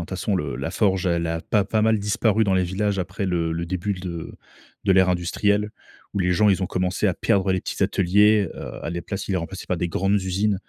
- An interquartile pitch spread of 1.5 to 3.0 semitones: Yes, narrow, 2.5 semitones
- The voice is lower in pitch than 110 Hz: Yes, very low, 95 Hz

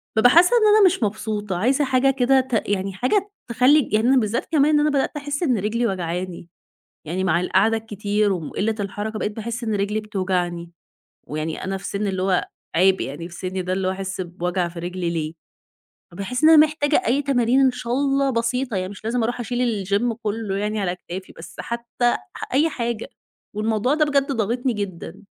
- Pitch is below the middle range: No, high, 215 Hz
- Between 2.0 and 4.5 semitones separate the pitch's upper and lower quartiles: No, average, 5.1 semitones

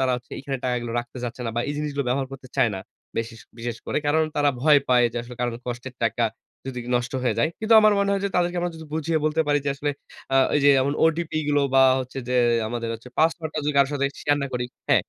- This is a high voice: No, medium, 140 Hz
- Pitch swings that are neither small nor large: Yes, average, 4.1 semitones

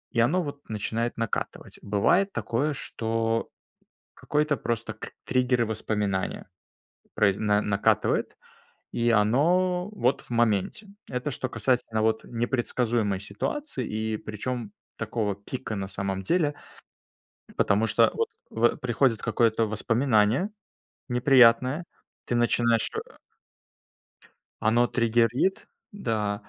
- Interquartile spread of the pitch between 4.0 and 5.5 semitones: No, average, 3.1 semitones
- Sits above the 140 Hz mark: No, low, 115 Hz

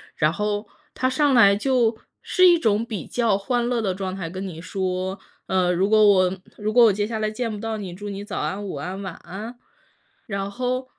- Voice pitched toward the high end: Yes, high, 205 Hz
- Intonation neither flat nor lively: Yes, average, 3.6 semitones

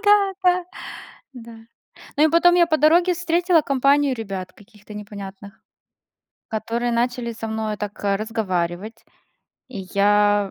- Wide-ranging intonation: Yes, wide, 6.8 semitones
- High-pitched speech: Yes, high, 225 Hz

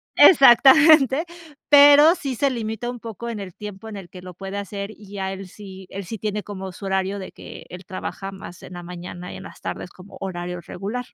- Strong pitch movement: No, average, 3.9 semitones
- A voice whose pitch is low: No, high, 200 Hz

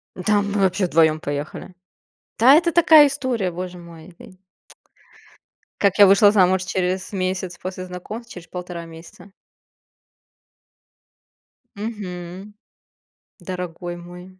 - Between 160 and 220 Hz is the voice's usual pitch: Yes, medium, 185 Hz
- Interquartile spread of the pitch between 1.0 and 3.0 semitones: Yes, narrow, 2.5 semitones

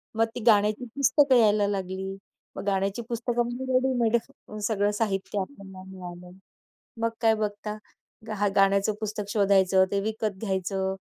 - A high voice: Yes, high, 205 Hz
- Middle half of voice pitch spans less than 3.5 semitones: Yes, average, 2.8 semitones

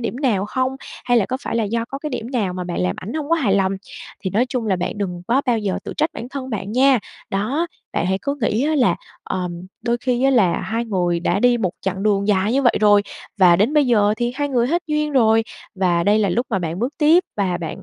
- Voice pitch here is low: No, high, 225 Hz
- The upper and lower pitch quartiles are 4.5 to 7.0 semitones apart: Yes, average, 5.2 semitones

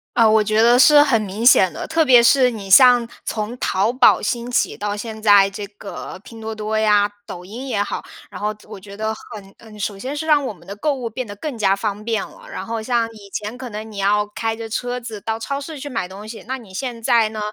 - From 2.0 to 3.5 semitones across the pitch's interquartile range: Yes, average, 3.0 semitones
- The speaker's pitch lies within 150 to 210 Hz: No, high, 220 Hz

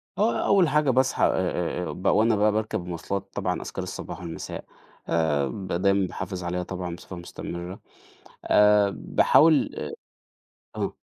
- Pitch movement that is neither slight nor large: Yes, average, 3.7 semitones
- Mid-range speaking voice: No, very low, 95 Hz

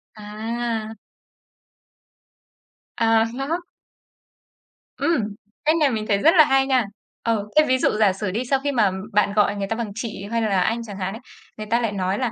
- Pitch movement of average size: Yes, average, 3.7 semitones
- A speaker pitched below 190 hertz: No, high, 225 Hz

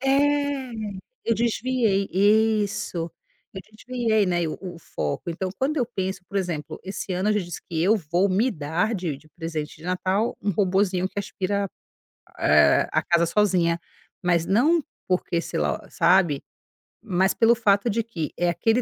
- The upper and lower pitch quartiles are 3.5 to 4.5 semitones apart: Yes, average, 4.2 semitones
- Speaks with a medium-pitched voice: No, high, 195 Hz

